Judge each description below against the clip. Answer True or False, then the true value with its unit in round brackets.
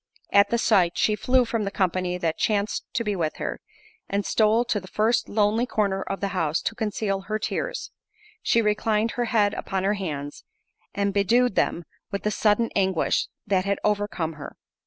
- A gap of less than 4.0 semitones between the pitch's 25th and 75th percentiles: True (2.6 semitones)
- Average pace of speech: True (180 wpm)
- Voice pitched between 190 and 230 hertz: True (205 Hz)